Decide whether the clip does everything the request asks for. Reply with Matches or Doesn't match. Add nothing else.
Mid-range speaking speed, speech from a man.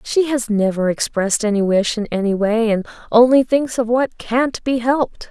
Doesn't match